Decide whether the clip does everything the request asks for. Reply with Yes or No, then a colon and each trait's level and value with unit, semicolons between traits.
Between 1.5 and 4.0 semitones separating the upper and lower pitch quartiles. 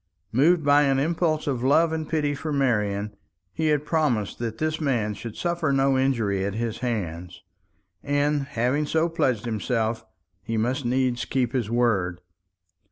No: average, 4.8 semitones